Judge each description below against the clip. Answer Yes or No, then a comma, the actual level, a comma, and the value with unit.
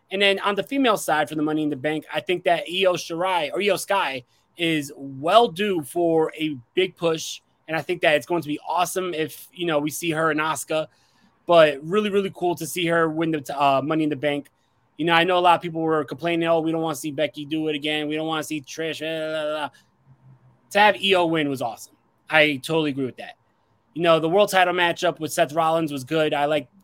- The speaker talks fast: Yes, fast, 255 wpm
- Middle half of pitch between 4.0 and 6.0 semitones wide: No, narrow, 2.5 semitones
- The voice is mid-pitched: Yes, medium, 160 Hz